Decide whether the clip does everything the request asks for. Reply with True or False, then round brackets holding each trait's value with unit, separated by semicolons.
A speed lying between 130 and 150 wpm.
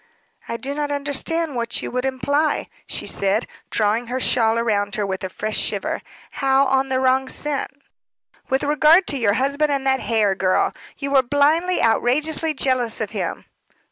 False (170 wpm)